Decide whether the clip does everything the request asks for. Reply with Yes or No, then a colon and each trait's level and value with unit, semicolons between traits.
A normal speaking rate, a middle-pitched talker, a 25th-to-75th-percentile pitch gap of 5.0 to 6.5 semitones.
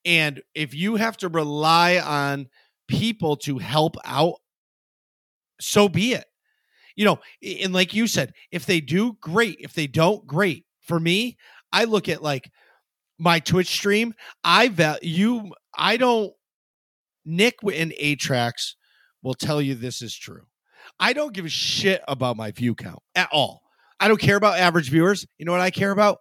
Yes: average, 170 wpm; medium, 175 Hz; wide, 5.4 semitones